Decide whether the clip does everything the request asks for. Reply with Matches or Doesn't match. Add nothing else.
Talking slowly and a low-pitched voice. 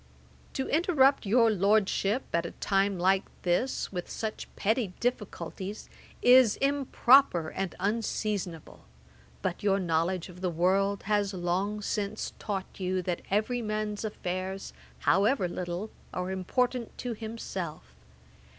Doesn't match